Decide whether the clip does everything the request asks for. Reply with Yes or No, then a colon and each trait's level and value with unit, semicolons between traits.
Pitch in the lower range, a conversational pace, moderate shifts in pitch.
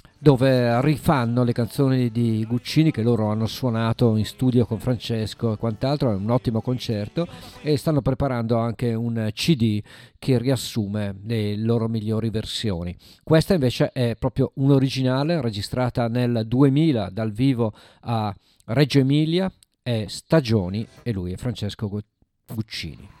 Yes: low, 120 Hz; average, 135 wpm; average, 3.4 semitones